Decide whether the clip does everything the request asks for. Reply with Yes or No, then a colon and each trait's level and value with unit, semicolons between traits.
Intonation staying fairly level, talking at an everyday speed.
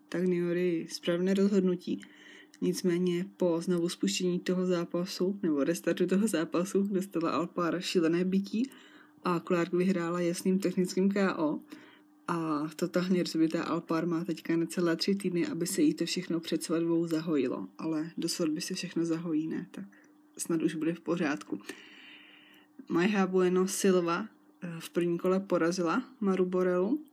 Yes: narrow, 2.2 semitones; average, 140 wpm